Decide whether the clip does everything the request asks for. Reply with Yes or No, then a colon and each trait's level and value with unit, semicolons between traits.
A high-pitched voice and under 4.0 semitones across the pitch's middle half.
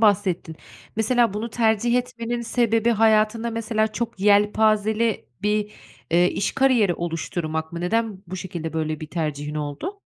No: high, 210 Hz; average, 4.8 semitones